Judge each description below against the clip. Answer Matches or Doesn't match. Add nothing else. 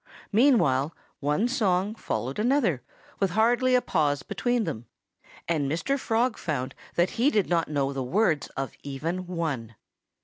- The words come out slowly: Doesn't match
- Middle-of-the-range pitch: Matches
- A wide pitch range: Matches